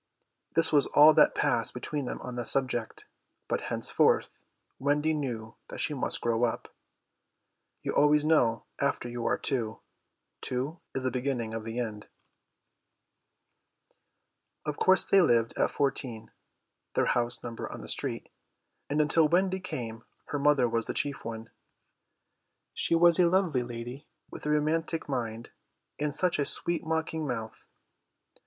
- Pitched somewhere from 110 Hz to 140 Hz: Yes, low, 135 Hz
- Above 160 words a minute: No, slow, 135 wpm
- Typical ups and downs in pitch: Yes, average, 4.6 semitones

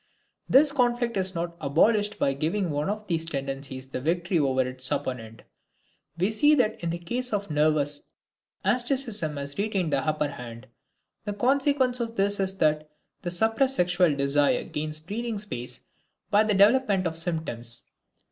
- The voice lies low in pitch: No, medium, 175 Hz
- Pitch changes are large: Yes, wide, 6.7 semitones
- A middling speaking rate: Yes, average, 160 wpm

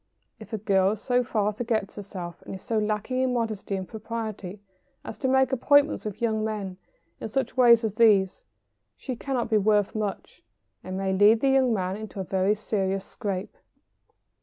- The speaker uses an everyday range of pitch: Yes, average, 3.2 semitones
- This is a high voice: Yes, high, 215 Hz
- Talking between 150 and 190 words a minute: Yes, average, 180 wpm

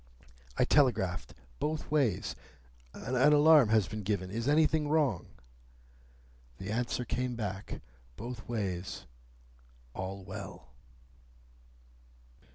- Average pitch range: No, wide, 6.3 semitones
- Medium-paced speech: No, slow, 95 wpm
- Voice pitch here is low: Yes, low, 110 Hz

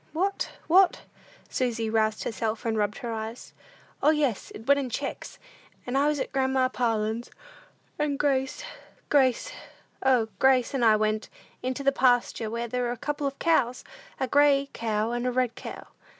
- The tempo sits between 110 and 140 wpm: No, average, 170 wpm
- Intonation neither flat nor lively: Yes, average, 3.4 semitones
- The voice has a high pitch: Yes, very high, 250 Hz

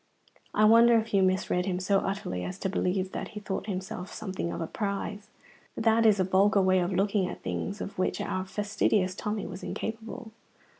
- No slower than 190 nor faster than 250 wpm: Yes, average, 195 wpm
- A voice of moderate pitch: No, high, 195 Hz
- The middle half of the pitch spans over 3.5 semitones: No, narrow, 2.4 semitones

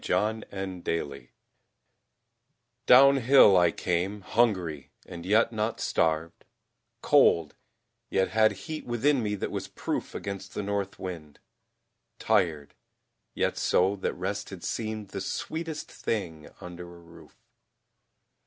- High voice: No, very low, 95 Hz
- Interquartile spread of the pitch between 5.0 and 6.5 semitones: No, average, 4.3 semitones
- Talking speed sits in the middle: No, slow, 115 wpm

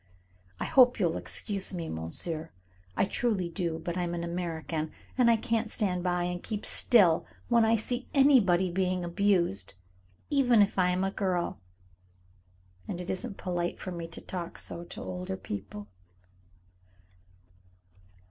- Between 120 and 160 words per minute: Yes, average, 150 wpm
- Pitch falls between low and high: Yes, medium, 180 Hz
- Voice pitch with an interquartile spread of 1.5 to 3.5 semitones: Yes, average, 3.2 semitones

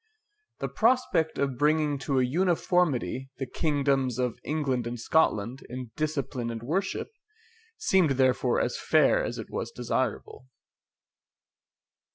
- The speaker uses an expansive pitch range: No, average, 3.9 semitones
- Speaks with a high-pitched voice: No, low, 135 Hz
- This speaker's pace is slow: Yes, slow, 125 wpm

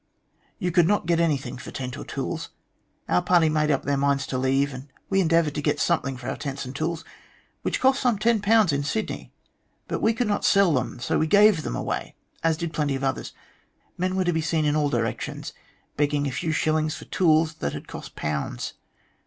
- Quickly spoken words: Yes, fast, 210 wpm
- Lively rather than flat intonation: No, average, 4.2 semitones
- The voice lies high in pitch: No, medium, 155 Hz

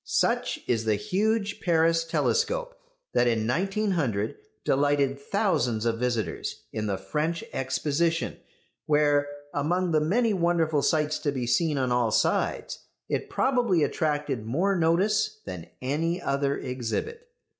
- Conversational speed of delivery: No, slow, 130 wpm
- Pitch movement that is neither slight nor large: No, wide, 6.4 semitones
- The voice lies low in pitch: No, medium, 150 Hz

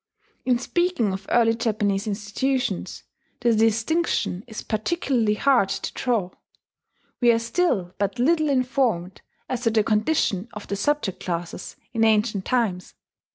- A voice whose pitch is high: Yes, high, 225 Hz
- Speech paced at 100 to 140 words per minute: Yes, slow, 135 wpm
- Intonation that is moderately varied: Yes, average, 3.9 semitones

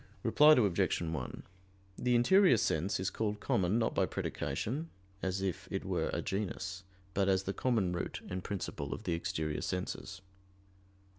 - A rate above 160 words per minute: No, average, 155 wpm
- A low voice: Yes, very low, 95 Hz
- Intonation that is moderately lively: Yes, average, 3.8 semitones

